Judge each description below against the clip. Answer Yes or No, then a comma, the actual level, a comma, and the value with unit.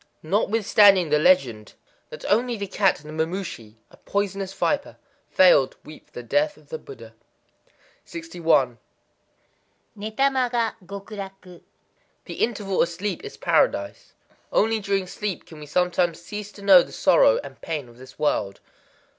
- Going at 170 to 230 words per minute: No, average, 150 wpm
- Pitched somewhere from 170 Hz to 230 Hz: Yes, high, 190 Hz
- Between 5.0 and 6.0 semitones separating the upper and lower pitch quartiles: Yes, average, 5.3 semitones